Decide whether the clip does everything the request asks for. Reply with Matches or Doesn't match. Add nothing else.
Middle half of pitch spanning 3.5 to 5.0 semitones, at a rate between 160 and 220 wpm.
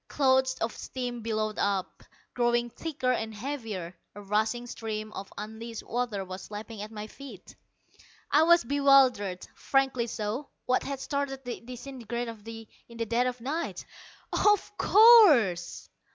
Doesn't match